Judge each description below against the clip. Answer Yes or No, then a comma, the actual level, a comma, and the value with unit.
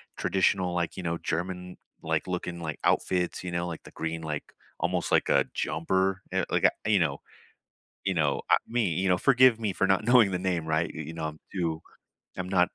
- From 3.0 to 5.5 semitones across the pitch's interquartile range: No, narrow, 2.6 semitones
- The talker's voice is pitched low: Yes, very low, 90 Hz